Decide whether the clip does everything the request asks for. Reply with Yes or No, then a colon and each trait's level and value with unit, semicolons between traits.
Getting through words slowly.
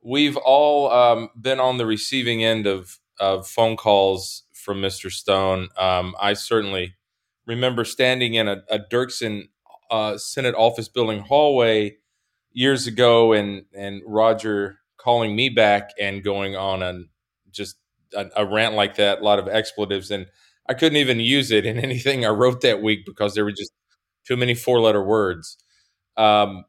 No: average, 165 wpm